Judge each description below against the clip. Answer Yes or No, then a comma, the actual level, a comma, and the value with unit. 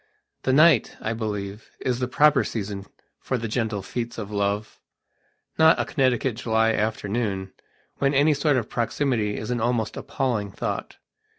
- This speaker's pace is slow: No, average, 155 wpm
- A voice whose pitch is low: Yes, low, 115 Hz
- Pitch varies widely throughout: No, average, 3.8 semitones